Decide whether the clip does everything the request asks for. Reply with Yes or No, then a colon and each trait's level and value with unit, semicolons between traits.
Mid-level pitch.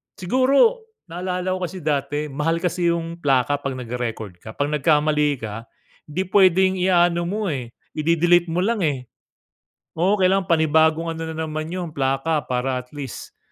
Yes: medium, 160 Hz